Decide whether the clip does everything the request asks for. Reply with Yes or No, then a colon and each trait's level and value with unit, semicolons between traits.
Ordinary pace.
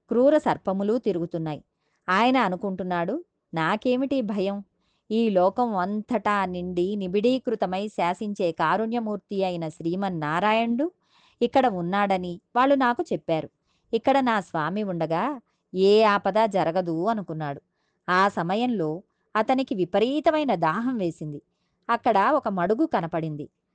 Yes: average, 100 wpm